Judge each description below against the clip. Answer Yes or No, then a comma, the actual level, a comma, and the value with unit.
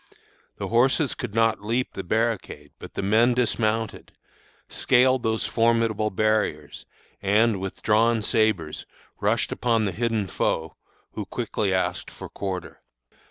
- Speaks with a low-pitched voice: Yes, low, 110 Hz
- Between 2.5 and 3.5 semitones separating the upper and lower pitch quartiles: Yes, average, 3.0 semitones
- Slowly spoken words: Yes, slow, 130 wpm